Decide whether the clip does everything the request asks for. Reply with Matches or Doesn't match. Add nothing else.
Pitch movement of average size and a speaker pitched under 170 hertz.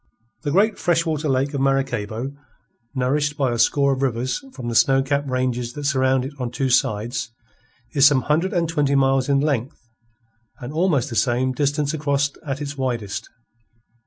Doesn't match